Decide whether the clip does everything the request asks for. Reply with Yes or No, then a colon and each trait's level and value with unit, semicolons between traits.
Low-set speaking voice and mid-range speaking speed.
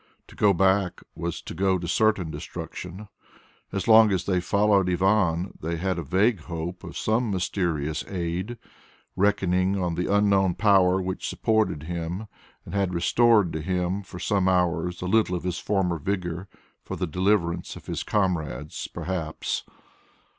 Yes: very low, 90 Hz; average, 155 wpm